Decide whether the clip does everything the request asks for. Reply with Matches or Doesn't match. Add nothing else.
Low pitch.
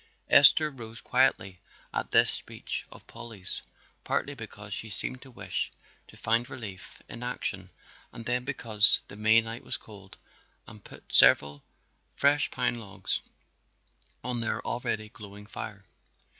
Matches